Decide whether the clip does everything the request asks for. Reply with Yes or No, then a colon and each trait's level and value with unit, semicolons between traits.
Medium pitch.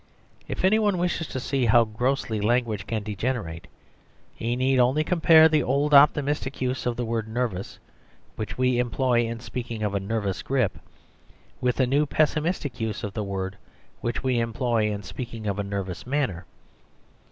No: low, 120 Hz